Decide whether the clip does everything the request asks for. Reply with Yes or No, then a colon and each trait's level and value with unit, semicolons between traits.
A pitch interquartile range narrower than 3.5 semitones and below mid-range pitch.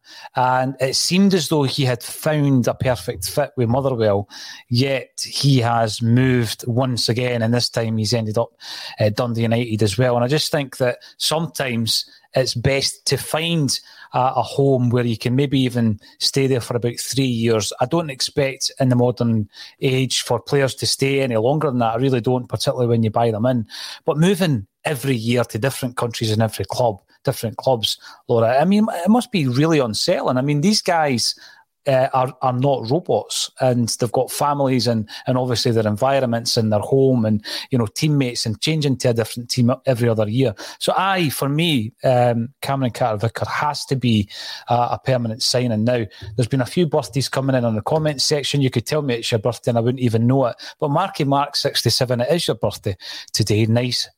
Yes: average, 2.7 semitones; low, 125 Hz